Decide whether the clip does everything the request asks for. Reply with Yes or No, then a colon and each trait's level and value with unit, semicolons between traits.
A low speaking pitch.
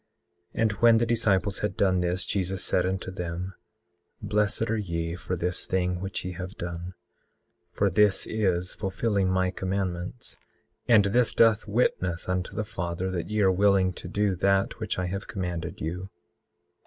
Yes: very low, 95 Hz